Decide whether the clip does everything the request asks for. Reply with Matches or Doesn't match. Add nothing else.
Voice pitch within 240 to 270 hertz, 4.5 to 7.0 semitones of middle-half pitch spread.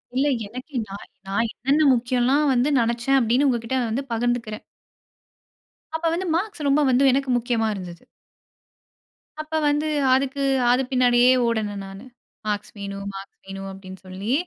Matches